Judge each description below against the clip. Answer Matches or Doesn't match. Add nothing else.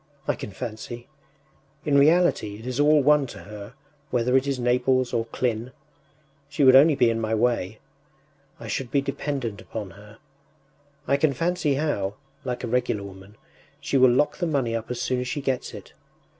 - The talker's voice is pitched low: Matches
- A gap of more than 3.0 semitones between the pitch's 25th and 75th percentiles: Matches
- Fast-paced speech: Doesn't match